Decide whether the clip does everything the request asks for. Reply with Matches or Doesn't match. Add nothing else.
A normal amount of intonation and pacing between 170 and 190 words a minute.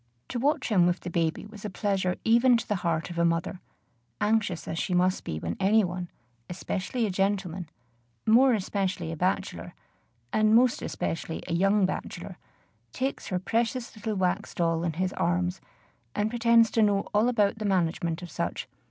Matches